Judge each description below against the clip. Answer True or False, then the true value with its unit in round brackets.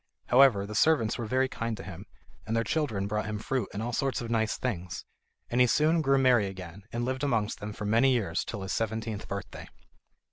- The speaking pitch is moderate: False (115 Hz)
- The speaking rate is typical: False (215 wpm)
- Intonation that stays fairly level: False (3.8 semitones)